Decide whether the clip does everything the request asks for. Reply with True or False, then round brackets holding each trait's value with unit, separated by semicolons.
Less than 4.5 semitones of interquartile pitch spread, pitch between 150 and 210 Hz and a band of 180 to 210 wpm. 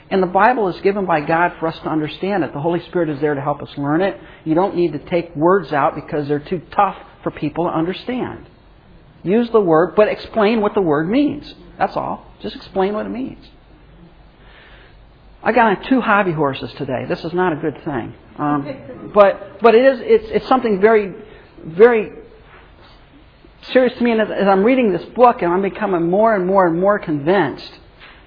False (4.9 semitones; 185 Hz; 200 wpm)